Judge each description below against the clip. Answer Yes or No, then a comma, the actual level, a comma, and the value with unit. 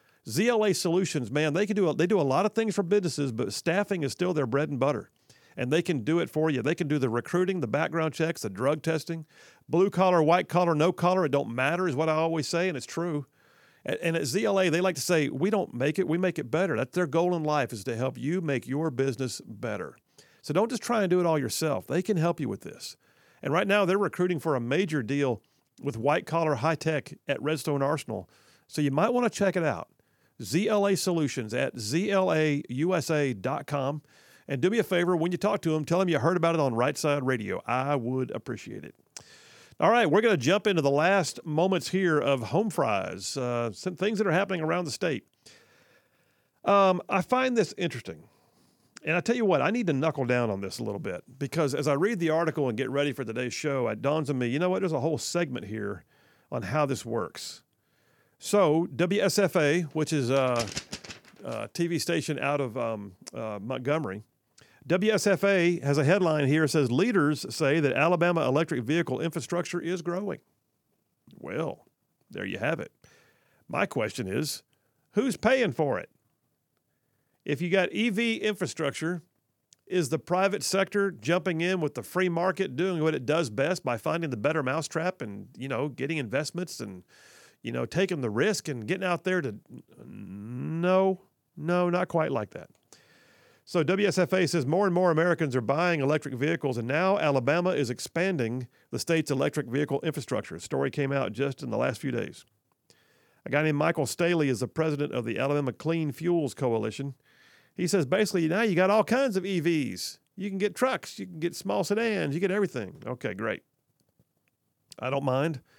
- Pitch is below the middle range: No, medium, 160 Hz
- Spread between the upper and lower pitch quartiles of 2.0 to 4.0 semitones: No, average, 4.6 semitones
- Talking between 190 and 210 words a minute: Yes, average, 200 wpm